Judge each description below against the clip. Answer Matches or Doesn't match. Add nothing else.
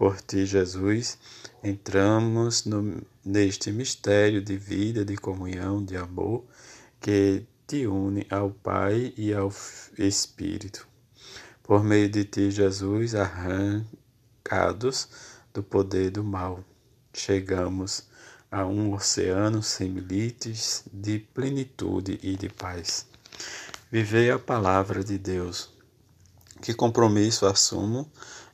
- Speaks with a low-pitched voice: Matches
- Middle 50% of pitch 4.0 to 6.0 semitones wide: Doesn't match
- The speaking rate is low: Matches